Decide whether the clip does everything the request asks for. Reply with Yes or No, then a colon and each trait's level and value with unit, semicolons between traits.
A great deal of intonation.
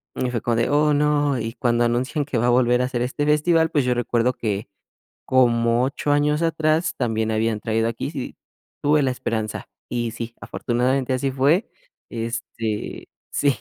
No: average, 3.8 semitones